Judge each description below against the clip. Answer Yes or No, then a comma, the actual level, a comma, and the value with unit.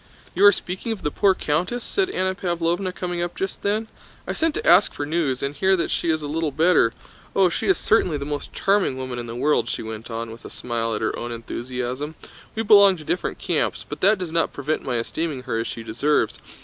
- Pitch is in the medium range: Yes, medium, 155 Hz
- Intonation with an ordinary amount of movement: No, wide, 6.8 semitones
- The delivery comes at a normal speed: No, fast, 235 wpm